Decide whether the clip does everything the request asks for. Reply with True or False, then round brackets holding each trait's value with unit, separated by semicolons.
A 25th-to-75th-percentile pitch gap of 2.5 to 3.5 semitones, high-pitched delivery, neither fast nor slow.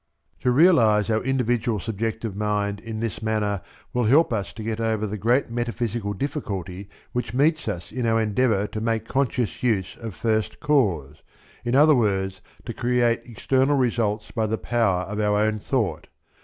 False (2.9 semitones; 110 Hz; 170 wpm)